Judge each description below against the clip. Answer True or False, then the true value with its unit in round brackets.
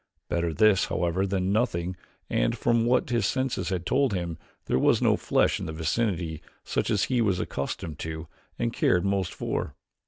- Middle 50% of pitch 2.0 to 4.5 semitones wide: False (5.1 semitones)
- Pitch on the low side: True (95 Hz)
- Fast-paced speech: False (180 wpm)